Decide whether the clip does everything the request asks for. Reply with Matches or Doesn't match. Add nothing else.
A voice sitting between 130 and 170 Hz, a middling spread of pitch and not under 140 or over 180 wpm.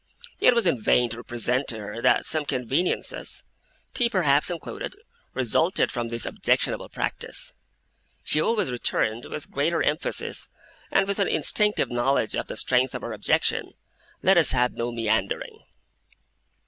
Doesn't match